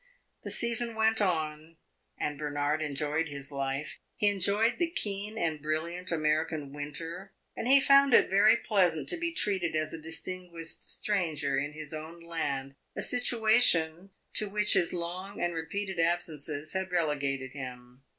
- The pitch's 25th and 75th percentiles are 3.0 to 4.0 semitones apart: No, average, 4.8 semitones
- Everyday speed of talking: Yes, average, 150 wpm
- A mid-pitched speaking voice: Yes, medium, 165 Hz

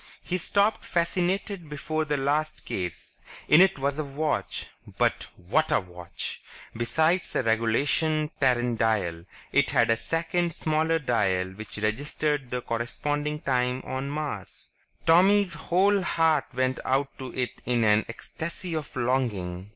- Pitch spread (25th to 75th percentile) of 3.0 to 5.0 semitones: No, wide, 5.6 semitones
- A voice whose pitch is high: No, medium, 140 Hz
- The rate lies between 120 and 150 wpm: Yes, average, 140 wpm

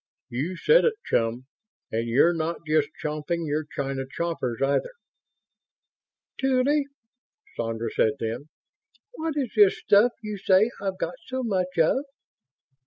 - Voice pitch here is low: No, medium, 170 Hz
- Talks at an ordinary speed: No, slow, 130 wpm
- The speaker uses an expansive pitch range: Yes, wide, 8.7 semitones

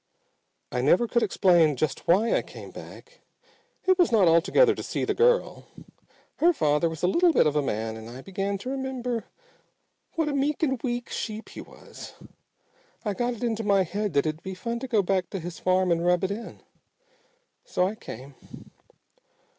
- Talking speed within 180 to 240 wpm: Yes, average, 190 wpm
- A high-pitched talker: Yes, high, 200 Hz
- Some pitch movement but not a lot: No, wide, 6.4 semitones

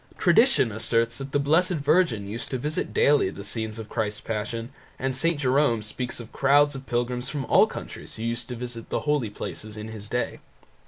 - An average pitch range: Yes, average, 4.3 semitones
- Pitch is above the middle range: No, low, 125 Hz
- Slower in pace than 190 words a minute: No, fast, 205 wpm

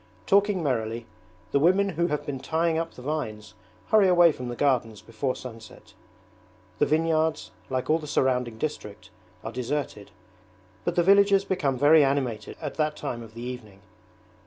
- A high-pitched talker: No, medium, 140 Hz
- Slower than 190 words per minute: Yes, average, 160 wpm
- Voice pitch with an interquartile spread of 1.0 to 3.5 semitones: No, wide, 5.6 semitones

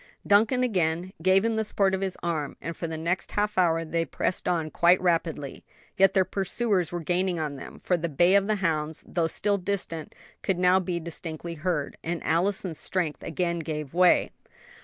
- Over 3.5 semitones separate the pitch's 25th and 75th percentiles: No, average, 2.7 semitones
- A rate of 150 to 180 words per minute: No, average, 190 wpm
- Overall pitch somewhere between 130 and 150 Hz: No, medium, 175 Hz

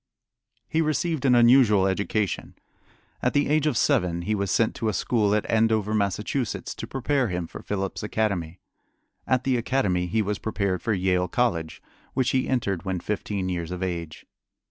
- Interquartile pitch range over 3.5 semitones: Yes, average, 5.0 semitones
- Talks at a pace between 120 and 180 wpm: Yes, average, 170 wpm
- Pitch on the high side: No, low, 105 Hz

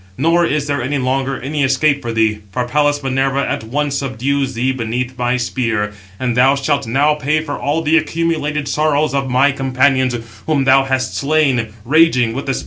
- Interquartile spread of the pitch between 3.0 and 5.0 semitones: No, narrow, 2.5 semitones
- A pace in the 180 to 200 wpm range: Yes, average, 190 wpm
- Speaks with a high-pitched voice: No, low, 135 Hz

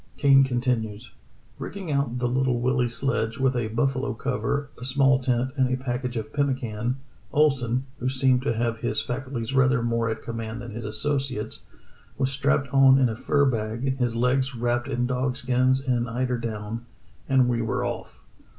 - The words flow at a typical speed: Yes, average, 175 wpm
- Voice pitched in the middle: No, low, 125 Hz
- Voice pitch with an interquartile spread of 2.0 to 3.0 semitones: Yes, narrow, 2.4 semitones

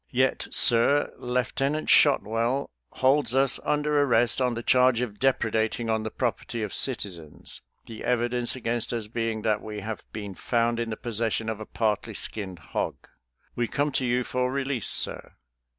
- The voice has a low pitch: Yes, low, 120 Hz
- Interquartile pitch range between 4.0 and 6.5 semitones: No, average, 2.8 semitones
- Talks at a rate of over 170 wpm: No, average, 165 wpm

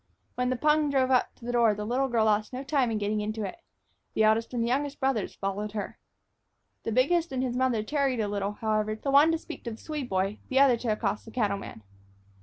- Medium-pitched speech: No, high, 235 Hz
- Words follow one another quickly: Yes, fast, 235 wpm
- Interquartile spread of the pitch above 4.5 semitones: No, average, 4.0 semitones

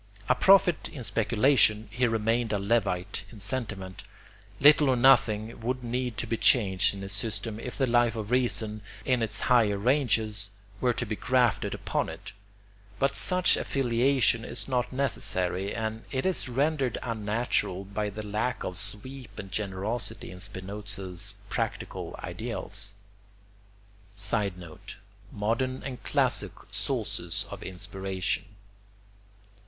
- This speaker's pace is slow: Yes, slow, 130 wpm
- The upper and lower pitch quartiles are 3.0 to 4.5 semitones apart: Yes, average, 3.8 semitones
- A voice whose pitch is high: No, low, 110 Hz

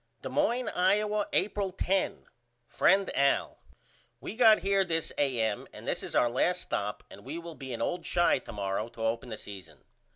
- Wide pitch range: Yes, wide, 9.0 semitones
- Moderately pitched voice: Yes, medium, 165 Hz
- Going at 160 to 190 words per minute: Yes, average, 185 wpm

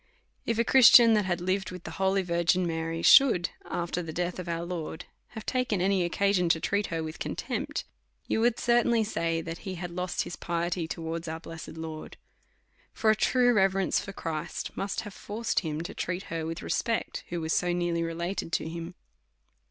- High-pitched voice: No, medium, 175 Hz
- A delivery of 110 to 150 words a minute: No, average, 190 wpm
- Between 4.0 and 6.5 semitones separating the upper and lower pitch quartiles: No, average, 3.2 semitones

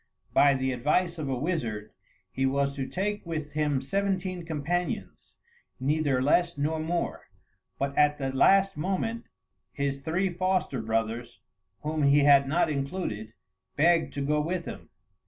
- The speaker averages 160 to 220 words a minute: No, average, 145 wpm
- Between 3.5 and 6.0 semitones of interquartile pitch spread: Yes, average, 4.3 semitones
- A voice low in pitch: No, medium, 150 Hz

